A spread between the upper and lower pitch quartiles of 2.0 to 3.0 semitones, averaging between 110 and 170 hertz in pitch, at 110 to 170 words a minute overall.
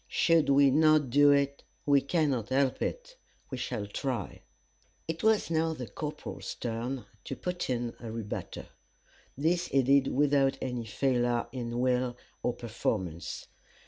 No: average, 3.4 semitones; low, 135 Hz; average, 145 wpm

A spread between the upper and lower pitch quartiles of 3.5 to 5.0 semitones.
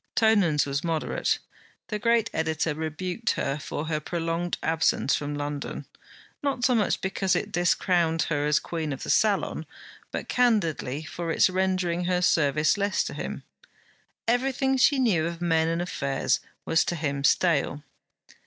Yes: average, 4.2 semitones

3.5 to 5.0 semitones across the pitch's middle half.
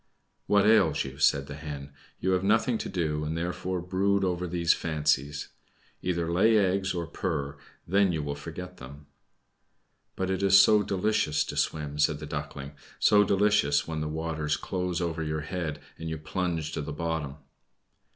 Yes: average, 3.8 semitones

